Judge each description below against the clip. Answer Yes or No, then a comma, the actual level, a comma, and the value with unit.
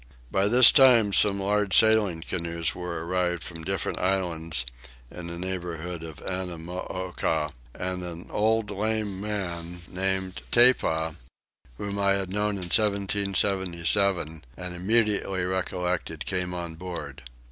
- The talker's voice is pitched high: No, very low, 90 Hz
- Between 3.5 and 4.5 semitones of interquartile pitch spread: No, average, 2.8 semitones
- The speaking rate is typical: No, slow, 125 wpm